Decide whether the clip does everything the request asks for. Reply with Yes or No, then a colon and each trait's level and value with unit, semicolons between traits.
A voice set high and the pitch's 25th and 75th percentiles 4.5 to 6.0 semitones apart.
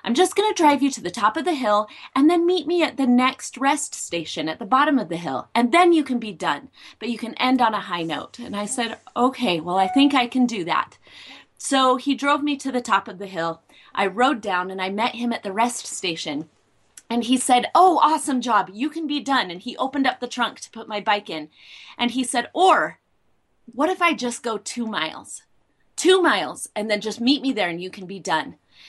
Yes: high, 245 Hz; average, 5.2 semitones